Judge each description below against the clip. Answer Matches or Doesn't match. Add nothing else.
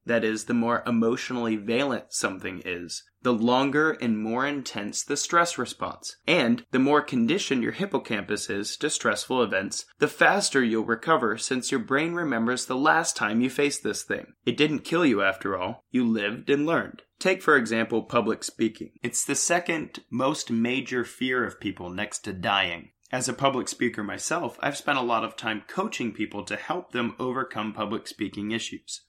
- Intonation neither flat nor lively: Matches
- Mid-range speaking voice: Doesn't match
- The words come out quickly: Doesn't match